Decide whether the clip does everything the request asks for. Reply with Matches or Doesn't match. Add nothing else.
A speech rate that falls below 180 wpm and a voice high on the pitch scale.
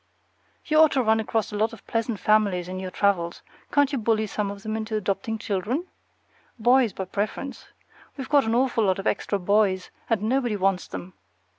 Doesn't match